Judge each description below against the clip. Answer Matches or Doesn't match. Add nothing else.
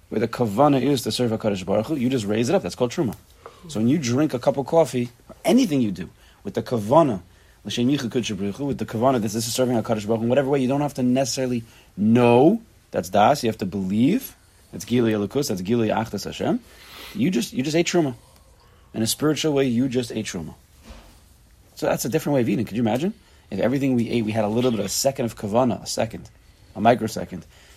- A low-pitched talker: Matches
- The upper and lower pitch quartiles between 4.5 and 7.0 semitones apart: Doesn't match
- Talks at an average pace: Doesn't match